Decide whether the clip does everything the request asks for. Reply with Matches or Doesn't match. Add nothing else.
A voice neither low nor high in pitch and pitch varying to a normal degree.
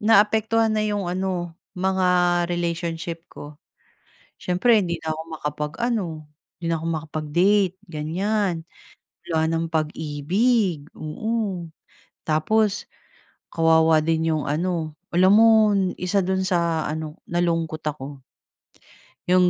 Matches